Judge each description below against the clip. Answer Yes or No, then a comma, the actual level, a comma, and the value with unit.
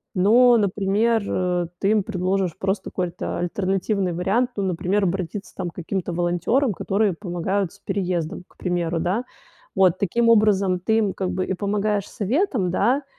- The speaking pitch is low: No, high, 190 Hz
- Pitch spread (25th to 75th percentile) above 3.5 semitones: No, average, 2.7 semitones